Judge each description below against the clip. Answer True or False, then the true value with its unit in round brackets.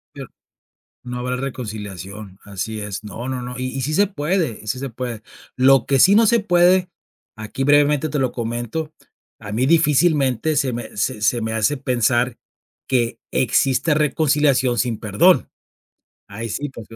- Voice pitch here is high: False (130 Hz)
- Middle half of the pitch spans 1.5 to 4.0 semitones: False (4.6 semitones)